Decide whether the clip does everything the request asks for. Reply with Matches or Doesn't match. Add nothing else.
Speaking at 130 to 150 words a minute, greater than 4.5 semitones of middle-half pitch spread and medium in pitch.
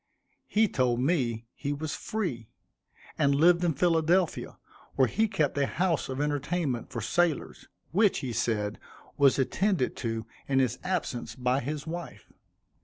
Matches